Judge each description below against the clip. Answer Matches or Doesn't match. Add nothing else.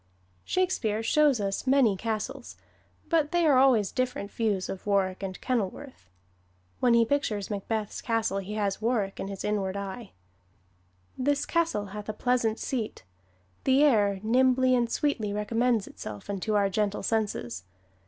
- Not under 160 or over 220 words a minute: Doesn't match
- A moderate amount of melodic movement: Matches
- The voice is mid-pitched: Doesn't match